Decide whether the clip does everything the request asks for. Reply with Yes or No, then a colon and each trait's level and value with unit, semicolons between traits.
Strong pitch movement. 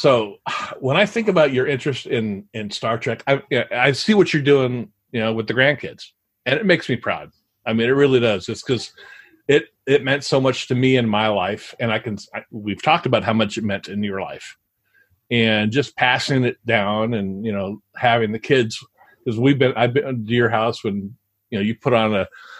No: average, 4.1 semitones